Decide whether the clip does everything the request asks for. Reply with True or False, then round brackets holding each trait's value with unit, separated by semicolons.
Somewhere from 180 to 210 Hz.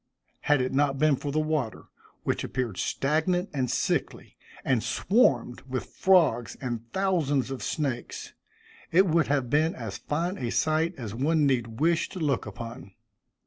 False (140 Hz)